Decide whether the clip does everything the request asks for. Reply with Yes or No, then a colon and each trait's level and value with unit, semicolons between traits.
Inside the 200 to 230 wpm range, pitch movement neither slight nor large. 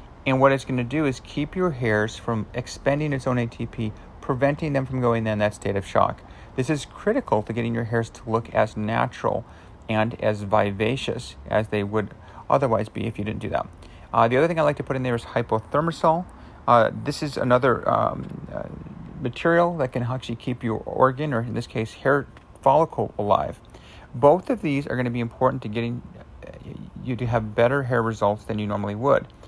Yes: fast, 205 wpm; average, 4.1 semitones